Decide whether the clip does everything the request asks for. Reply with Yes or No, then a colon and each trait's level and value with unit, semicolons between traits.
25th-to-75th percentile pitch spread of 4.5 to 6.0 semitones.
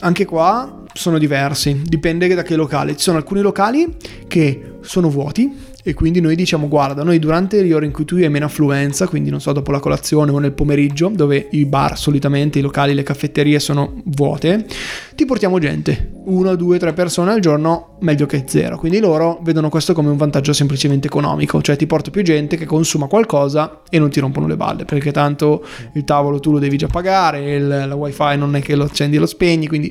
No: average, 3.1 semitones